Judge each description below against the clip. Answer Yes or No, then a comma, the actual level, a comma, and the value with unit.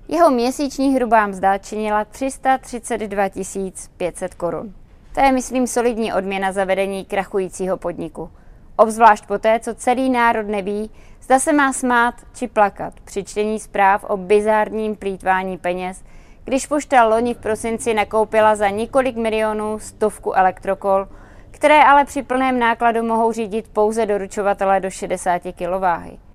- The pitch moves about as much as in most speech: Yes, average, 3.6 semitones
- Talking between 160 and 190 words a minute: No, average, 135 wpm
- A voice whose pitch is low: No, high, 215 Hz